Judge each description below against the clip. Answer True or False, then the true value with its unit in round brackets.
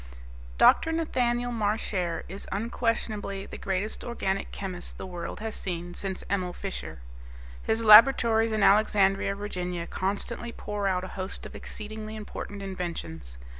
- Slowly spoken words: True (130 wpm)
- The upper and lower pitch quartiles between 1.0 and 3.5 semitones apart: True (2.9 semitones)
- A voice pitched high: True (200 Hz)